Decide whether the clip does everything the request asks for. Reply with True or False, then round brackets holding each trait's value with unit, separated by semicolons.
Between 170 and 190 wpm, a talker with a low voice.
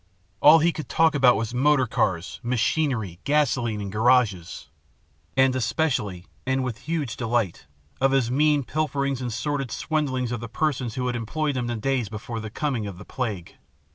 True (175 wpm; 125 Hz)